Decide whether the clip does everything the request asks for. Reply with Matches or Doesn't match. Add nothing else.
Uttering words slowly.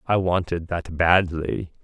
Matches